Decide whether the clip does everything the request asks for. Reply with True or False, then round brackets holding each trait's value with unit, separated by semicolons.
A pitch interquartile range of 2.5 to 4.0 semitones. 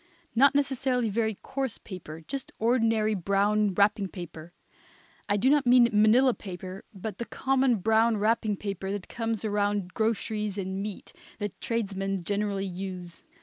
True (3.0 semitones)